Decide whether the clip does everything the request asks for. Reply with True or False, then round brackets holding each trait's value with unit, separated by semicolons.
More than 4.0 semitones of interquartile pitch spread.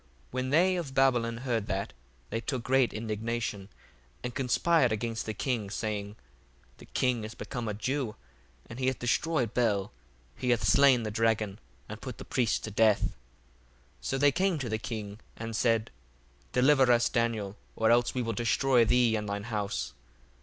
False (2.9 semitones)